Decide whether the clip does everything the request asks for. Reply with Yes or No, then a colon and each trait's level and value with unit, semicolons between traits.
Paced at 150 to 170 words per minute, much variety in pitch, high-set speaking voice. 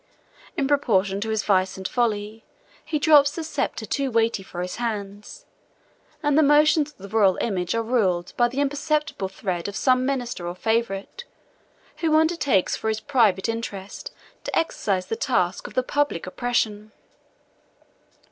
Yes: average, 155 wpm; wide, 6.2 semitones; high, 225 Hz